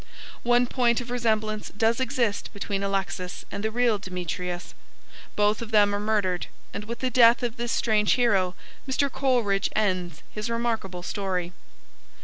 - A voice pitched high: Yes, high, 215 Hz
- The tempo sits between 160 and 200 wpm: No, average, 150 wpm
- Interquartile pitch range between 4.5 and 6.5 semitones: No, average, 3.4 semitones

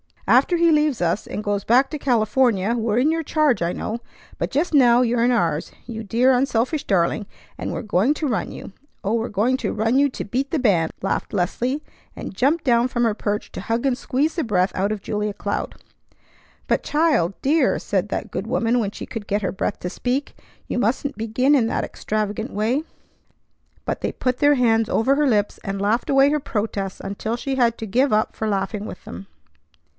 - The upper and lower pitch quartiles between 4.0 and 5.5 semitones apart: Yes, average, 4.4 semitones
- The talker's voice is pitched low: No, high, 230 Hz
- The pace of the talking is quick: Yes, fast, 210 wpm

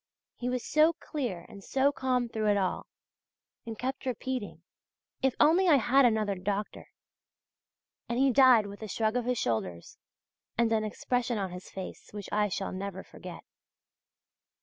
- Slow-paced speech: No, average, 160 wpm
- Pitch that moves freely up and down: No, average, 4.2 semitones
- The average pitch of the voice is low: No, high, 225 Hz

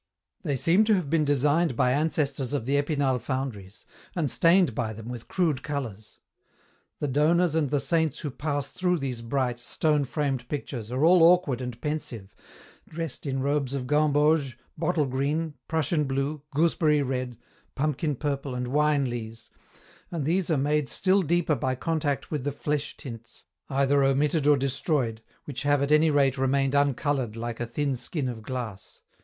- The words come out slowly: No, average, 170 wpm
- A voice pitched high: No, medium, 140 Hz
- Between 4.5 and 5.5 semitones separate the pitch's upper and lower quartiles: No, average, 3.0 semitones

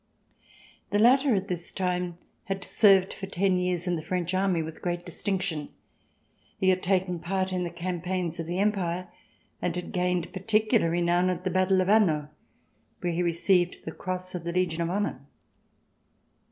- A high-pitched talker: No, medium, 180 Hz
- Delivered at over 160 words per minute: Yes, average, 170 wpm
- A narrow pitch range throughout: Yes, narrow, 1.7 semitones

